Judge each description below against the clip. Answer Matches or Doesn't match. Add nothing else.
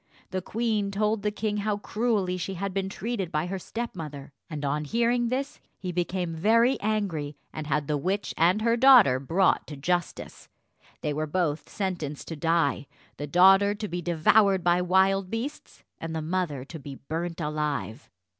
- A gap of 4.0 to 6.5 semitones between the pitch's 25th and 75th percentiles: Matches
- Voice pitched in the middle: Matches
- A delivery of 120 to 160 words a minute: Doesn't match